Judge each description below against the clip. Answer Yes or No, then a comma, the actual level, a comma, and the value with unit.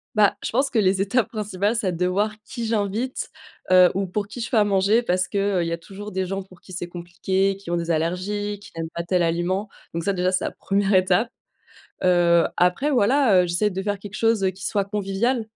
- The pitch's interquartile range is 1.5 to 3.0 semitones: Yes, narrow, 2.6 semitones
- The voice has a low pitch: No, high, 195 Hz